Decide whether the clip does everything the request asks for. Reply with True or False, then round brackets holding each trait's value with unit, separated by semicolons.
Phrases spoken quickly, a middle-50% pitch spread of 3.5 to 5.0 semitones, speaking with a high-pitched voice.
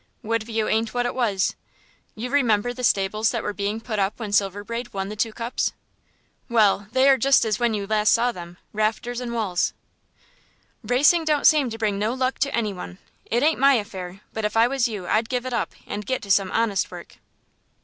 False (210 wpm; 3.0 semitones; 225 Hz)